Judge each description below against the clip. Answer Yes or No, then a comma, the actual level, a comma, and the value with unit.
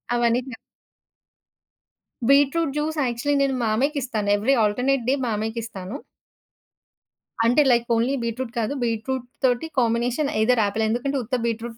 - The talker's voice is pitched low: No, high, 240 Hz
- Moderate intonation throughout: Yes, average, 3.1 semitones